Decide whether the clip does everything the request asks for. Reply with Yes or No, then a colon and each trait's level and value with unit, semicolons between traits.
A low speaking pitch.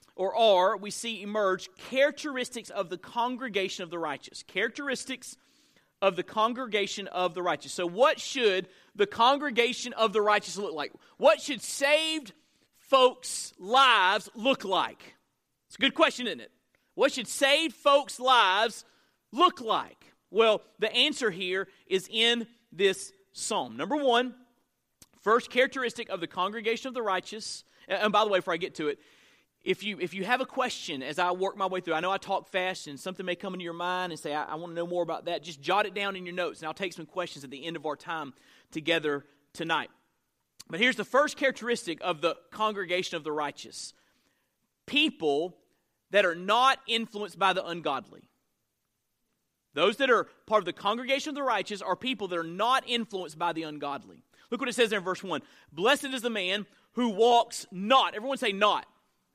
No: high, 205 Hz